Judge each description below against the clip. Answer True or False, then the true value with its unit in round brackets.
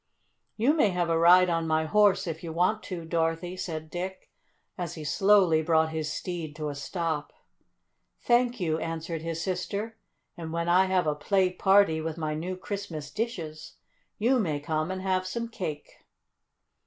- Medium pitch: True (170 Hz)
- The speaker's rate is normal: True (170 wpm)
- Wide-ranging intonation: False (3.1 semitones)